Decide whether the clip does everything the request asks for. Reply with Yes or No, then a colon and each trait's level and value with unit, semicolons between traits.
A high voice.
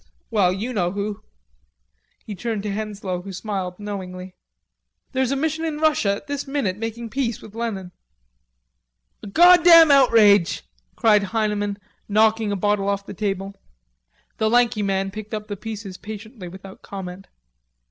Yes: high, 210 Hz